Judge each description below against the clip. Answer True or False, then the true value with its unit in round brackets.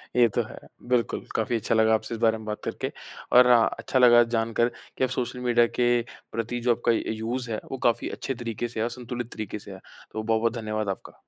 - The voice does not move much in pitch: True (1.5 semitones)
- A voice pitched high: False (115 Hz)